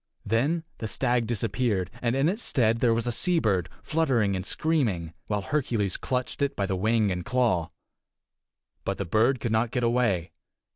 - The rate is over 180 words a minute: No, average, 175 wpm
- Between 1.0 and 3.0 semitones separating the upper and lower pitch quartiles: No, average, 4.3 semitones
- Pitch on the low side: Yes, low, 115 Hz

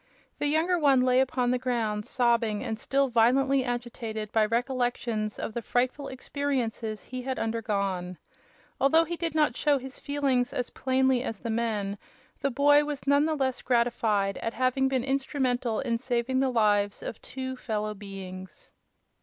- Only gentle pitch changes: No, average, 3.2 semitones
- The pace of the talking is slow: No, average, 160 wpm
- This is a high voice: Yes, high, 245 Hz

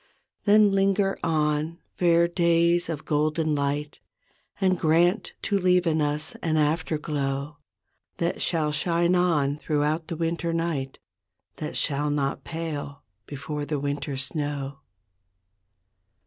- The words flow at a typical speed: No, slow, 120 wpm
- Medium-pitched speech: Yes, medium, 155 Hz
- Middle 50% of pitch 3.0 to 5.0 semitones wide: No, narrow, 2.6 semitones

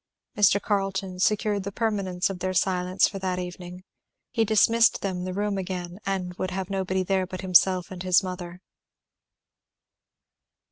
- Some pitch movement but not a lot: No, narrow, 1.4 semitones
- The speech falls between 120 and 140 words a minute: No, average, 150 wpm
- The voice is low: No, medium, 185 Hz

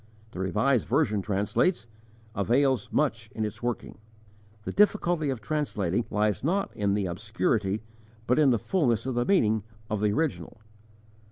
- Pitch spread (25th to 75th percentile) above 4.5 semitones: Yes, average, 5.2 semitones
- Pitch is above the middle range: No, low, 115 Hz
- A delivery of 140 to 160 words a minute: Yes, average, 150 wpm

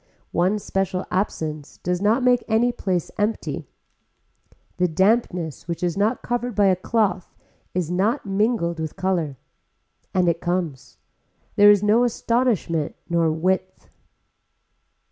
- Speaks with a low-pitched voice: No, high, 190 Hz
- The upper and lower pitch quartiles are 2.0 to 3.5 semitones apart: No, average, 4.0 semitones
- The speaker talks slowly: Yes, slow, 125 wpm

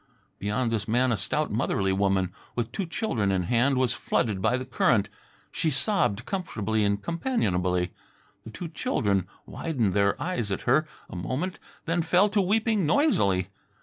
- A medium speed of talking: Yes, average, 160 wpm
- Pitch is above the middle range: No, low, 115 Hz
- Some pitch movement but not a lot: No, wide, 8.8 semitones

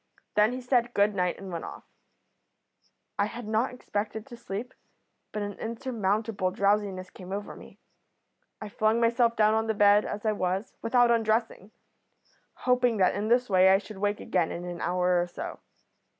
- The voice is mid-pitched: No, high, 210 Hz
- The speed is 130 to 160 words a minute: No, average, 175 wpm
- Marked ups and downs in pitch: No, average, 3.0 semitones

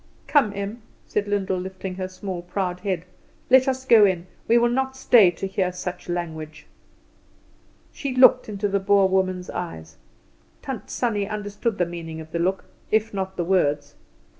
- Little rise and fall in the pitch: No, average, 3.1 semitones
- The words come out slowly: No, average, 165 wpm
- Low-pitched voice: No, high, 190 Hz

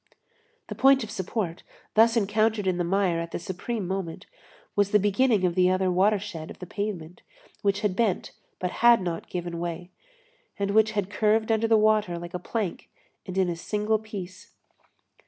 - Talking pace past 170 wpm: Yes, average, 180 wpm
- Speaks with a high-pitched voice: Yes, high, 195 Hz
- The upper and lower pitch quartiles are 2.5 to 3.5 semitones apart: Yes, average, 3.2 semitones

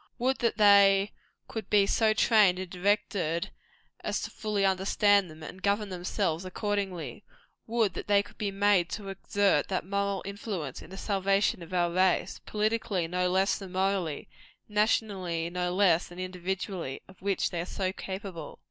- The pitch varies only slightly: Yes, narrow, 2.1 semitones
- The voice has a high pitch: Yes, high, 195 Hz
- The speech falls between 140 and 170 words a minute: Yes, average, 165 wpm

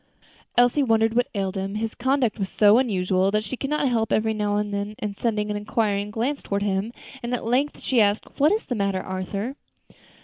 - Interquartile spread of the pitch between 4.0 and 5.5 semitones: No, average, 3.3 semitones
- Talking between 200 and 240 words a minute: Yes, fast, 205 wpm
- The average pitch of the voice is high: Yes, high, 215 Hz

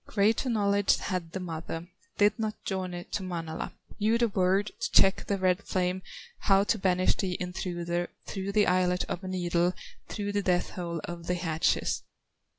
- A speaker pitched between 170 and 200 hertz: Yes, medium, 185 Hz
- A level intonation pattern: Yes, narrow, 2.3 semitones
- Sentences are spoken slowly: No, average, 170 wpm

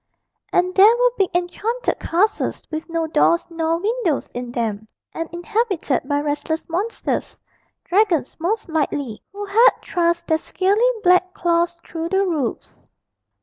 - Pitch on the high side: Yes, very high, 345 Hz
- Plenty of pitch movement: No, average, 3.9 semitones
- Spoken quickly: No, average, 140 wpm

